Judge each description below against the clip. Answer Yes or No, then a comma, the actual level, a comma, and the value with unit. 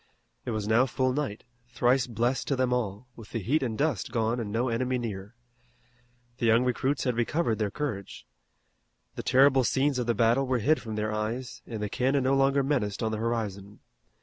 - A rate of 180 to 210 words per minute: Yes, average, 200 wpm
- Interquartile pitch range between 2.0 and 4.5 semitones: Yes, average, 3.1 semitones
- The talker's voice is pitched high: No, low, 120 Hz